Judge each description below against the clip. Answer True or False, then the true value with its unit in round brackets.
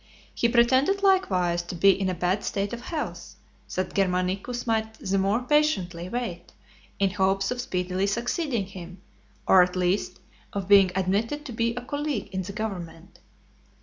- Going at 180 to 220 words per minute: False (165 wpm)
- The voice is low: False (195 Hz)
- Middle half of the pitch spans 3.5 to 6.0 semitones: True (4.5 semitones)